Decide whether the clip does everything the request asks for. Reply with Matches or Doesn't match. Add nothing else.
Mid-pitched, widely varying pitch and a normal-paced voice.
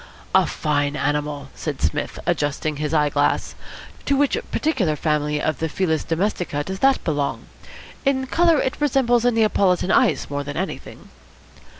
Matches